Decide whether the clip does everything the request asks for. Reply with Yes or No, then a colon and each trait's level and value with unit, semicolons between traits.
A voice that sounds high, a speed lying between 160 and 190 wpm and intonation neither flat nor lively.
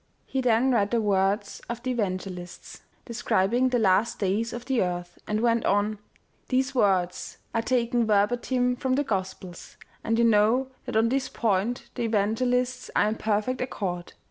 Yes: high, 225 Hz; average, 170 wpm; average, 3.8 semitones